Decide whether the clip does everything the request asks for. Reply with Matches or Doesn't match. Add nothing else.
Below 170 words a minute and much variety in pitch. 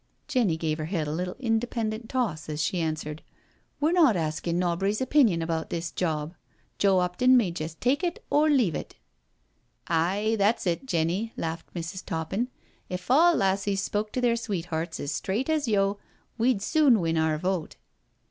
Doesn't match